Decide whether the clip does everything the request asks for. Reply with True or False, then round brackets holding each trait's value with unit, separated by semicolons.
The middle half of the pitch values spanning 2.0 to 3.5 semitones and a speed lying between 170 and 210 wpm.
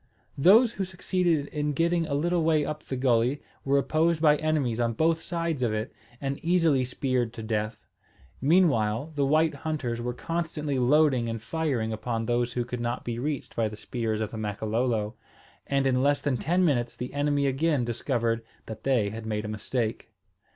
False (5.1 semitones; 185 wpm)